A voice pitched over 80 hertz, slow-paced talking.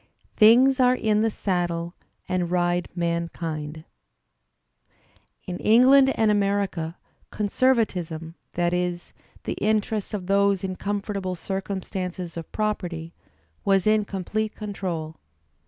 Yes: high, 190 Hz; slow, 105 wpm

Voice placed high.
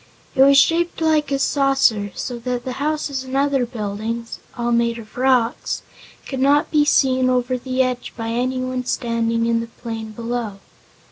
Yes: very high, 250 Hz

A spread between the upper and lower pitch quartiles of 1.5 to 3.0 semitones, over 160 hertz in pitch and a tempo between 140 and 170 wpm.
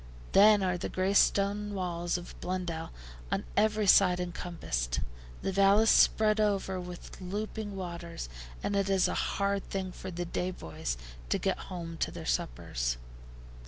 Yes: narrow, 2.5 semitones; medium, 185 Hz; average, 160 wpm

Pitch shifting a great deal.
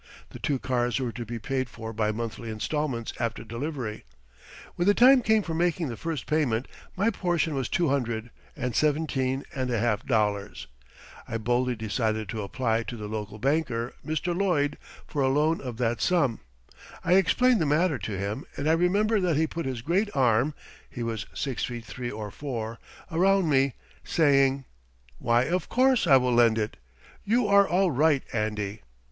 Yes: wide, 6.0 semitones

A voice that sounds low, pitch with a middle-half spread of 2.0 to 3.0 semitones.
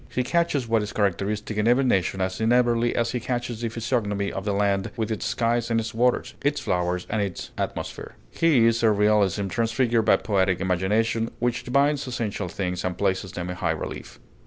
No: low, 110 Hz; average, 3.6 semitones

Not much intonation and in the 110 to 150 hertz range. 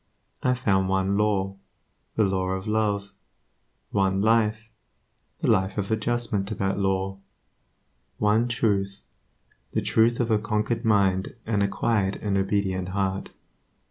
No: narrow, 2.2 semitones; low, 100 Hz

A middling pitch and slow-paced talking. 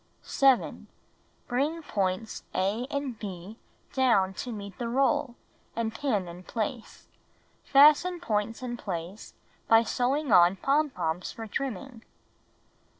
No: high, 230 Hz; slow, 120 wpm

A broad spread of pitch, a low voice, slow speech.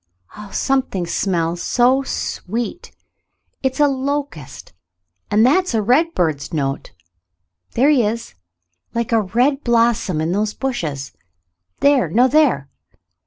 No: wide, 7.2 semitones; high, 230 Hz; slow, 120 wpm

